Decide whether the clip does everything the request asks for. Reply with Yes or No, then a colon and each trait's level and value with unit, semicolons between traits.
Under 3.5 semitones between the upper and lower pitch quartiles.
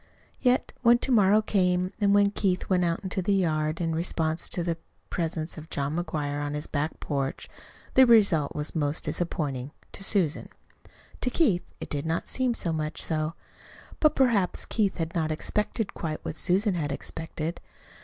No: average, 4.5 semitones